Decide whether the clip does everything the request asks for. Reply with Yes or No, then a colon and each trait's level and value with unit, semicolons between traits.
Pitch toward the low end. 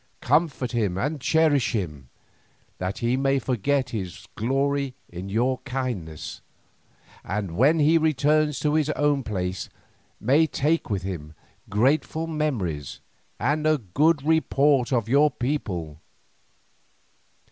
Yes: low, 130 Hz